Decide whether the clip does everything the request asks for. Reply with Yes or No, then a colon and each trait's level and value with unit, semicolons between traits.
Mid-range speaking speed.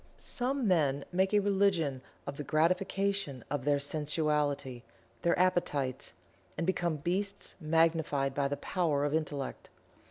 No: slow, 130 wpm